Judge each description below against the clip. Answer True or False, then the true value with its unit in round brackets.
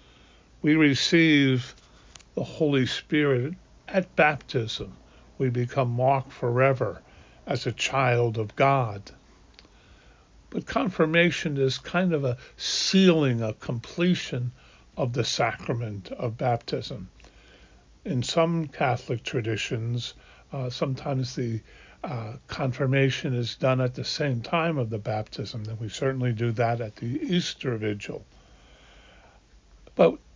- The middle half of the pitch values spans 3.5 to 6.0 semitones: True (3.9 semitones)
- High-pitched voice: False (125 Hz)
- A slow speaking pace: True (115 wpm)